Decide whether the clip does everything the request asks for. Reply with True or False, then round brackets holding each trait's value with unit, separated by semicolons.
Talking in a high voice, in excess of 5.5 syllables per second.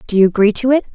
True (225 Hz; 8.1 syllables/s)